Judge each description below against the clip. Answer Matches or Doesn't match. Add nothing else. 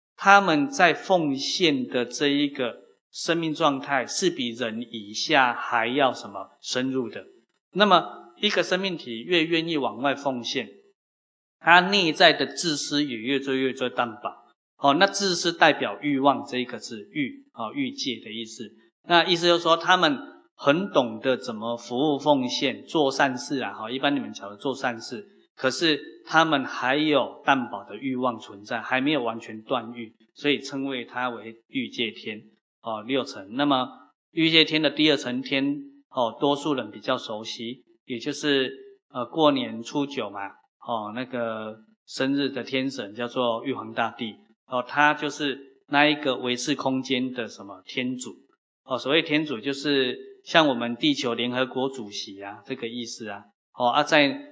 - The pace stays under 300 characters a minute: Matches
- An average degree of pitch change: Matches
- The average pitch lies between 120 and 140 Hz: Matches